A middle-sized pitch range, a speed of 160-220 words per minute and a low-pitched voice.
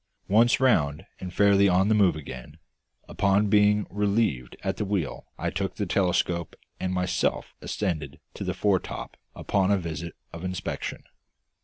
No: average, 3.3 semitones; average, 150 wpm; very low, 95 Hz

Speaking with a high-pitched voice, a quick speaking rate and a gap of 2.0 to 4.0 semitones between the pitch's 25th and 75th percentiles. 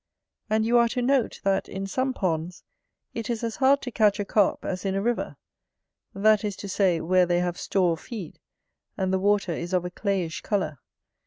Yes: high, 195 Hz; fast, 210 wpm; average, 3.6 semitones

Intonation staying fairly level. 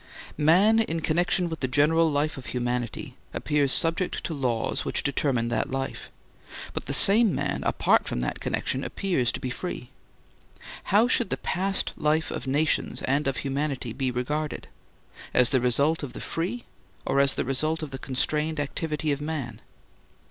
No: average, 3.7 semitones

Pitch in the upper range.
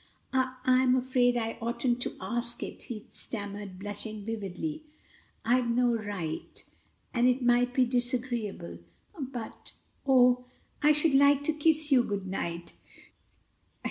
Yes: high, 245 Hz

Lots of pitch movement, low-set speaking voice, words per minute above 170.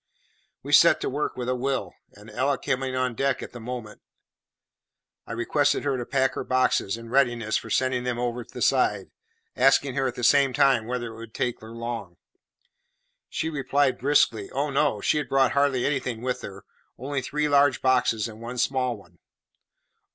No: average, 2.7 semitones; low, 125 Hz; average, 185 wpm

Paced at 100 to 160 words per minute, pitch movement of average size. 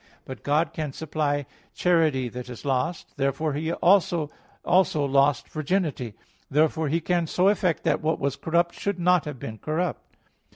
Yes: average, 150 wpm; average, 3.6 semitones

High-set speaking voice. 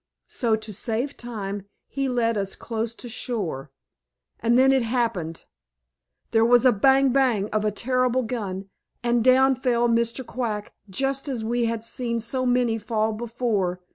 Yes: high, 235 Hz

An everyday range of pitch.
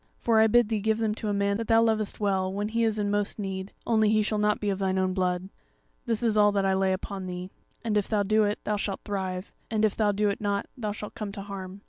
No: narrow, 1.9 semitones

